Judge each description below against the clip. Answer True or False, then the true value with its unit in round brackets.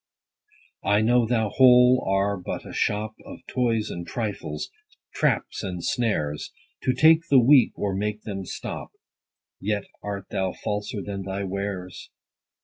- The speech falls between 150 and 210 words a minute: False (140 wpm)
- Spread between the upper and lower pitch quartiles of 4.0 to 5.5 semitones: False (3.4 semitones)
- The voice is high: False (105 Hz)